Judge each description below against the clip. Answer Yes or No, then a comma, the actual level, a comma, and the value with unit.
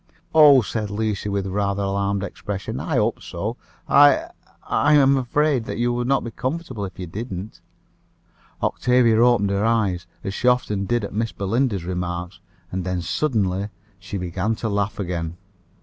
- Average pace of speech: Yes, average, 165 wpm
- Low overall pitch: Yes, low, 105 Hz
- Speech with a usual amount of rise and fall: Yes, average, 4.0 semitones